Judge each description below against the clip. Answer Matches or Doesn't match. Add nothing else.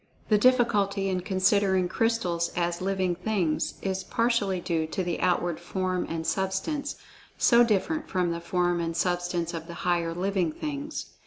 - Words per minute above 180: Doesn't match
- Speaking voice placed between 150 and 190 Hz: Matches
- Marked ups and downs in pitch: Doesn't match